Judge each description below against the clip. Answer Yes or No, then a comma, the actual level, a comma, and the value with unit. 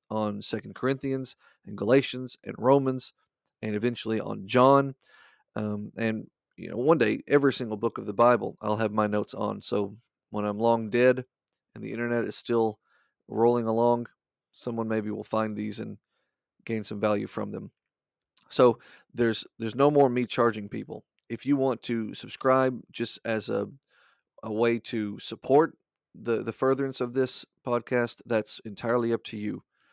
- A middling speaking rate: Yes, average, 165 wpm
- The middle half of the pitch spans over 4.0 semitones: No, average, 2.7 semitones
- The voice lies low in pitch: Yes, low, 115 Hz